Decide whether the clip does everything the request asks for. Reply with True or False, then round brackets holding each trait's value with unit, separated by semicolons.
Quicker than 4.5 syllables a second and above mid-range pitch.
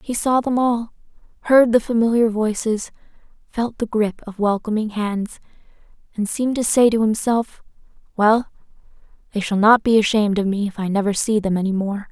True (5.3 syllables/s; 220 Hz)